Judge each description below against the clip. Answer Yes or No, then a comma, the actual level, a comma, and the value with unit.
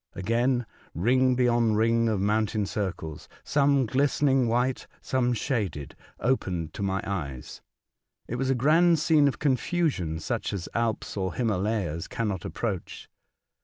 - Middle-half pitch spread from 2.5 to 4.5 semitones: No, average, 5.2 semitones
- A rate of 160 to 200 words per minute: No, average, 140 wpm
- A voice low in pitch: Yes, low, 115 Hz